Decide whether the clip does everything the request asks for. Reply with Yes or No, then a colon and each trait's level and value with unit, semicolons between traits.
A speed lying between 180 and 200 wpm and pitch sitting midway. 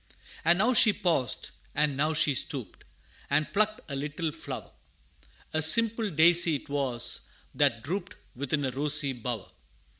No: average, 140 wpm; medium, 150 Hz